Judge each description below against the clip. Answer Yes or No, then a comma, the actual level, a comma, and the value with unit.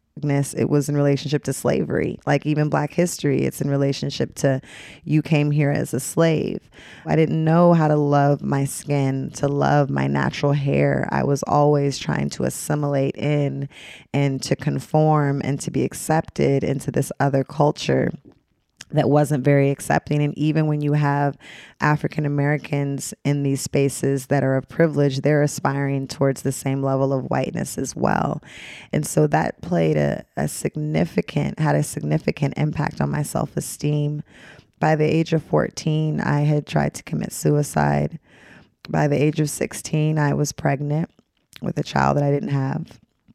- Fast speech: No, average, 165 wpm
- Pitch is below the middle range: No, medium, 145 Hz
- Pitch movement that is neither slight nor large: No, narrow, 1.7 semitones